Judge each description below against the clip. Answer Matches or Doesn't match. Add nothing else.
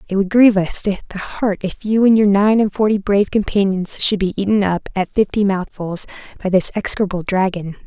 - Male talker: Doesn't match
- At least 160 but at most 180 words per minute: Doesn't match